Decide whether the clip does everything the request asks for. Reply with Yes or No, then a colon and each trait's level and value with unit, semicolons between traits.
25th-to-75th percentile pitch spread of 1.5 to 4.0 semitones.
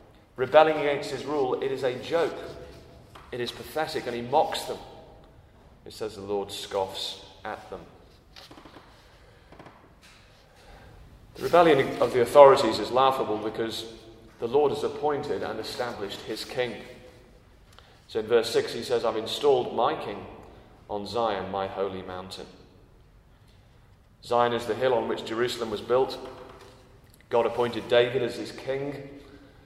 No: average, 4.8 semitones